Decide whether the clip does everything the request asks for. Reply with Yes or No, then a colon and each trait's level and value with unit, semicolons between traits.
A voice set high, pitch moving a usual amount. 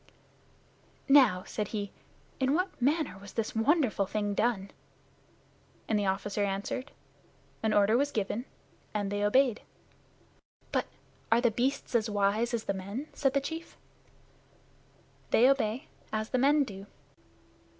Yes: high, 225 Hz; average, 4.7 semitones